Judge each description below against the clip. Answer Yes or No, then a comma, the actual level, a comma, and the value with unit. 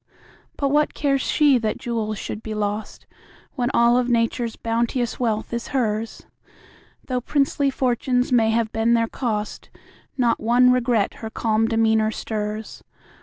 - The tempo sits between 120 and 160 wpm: Yes, average, 145 wpm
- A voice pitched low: No, high, 235 Hz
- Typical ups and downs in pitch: No, narrow, 2.2 semitones